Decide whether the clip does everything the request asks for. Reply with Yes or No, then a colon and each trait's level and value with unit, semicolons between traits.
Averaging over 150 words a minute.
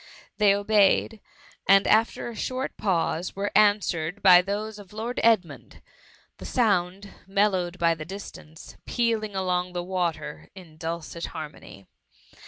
No: slow, 135 wpm